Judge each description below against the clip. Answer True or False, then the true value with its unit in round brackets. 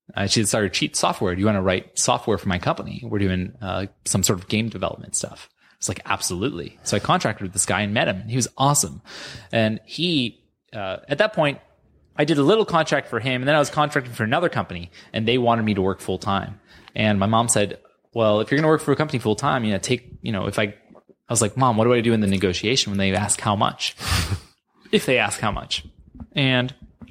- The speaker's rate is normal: False (250 wpm)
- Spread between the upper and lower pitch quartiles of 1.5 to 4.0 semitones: False (4.7 semitones)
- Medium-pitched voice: False (110 Hz)